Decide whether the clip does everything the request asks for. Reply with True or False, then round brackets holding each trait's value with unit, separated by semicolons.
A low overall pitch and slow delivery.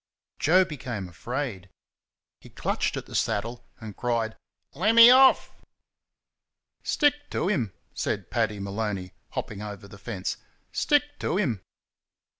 True (115 Hz; 125 wpm)